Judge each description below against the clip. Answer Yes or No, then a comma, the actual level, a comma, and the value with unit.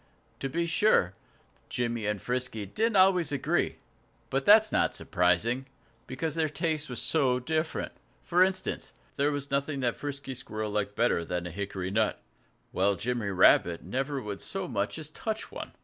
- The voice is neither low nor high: No, low, 130 Hz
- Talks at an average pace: Yes, average, 170 wpm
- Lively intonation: Yes, wide, 7.2 semitones